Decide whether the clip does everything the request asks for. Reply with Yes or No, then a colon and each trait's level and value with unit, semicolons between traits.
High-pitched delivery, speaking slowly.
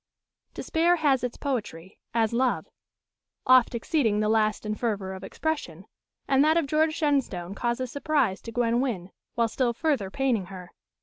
No: high, 235 Hz; average, 160 wpm